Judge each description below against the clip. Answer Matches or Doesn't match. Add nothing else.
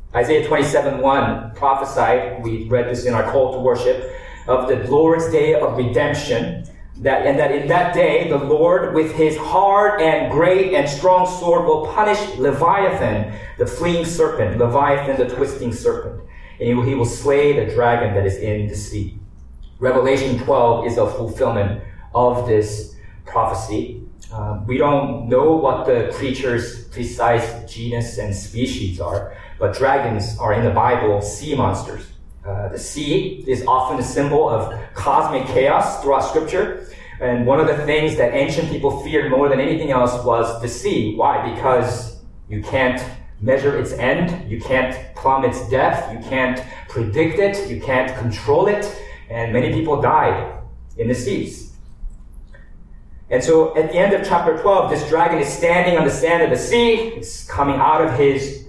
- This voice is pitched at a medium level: Doesn't match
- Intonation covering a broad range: Matches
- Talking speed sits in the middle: Matches